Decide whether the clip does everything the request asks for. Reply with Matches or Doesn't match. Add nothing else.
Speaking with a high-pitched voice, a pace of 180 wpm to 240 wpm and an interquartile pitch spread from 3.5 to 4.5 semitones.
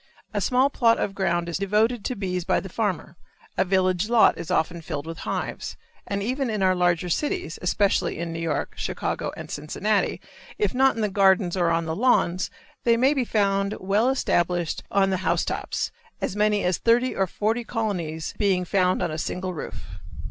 Matches